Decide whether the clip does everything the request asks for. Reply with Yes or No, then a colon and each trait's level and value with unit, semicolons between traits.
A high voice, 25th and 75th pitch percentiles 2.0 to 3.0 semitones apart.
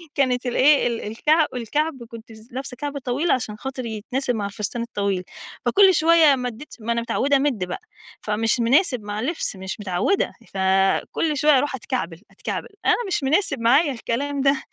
No: very high, 250 Hz; average, 4.7 semitones